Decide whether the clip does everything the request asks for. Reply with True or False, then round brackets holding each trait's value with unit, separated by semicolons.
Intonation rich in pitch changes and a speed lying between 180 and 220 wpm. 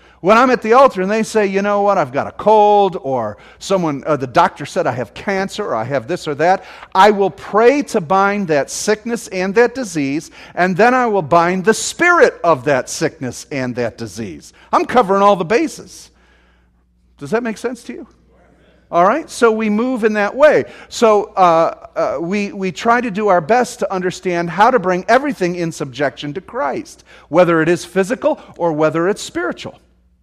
True (5.9 semitones; 200 wpm)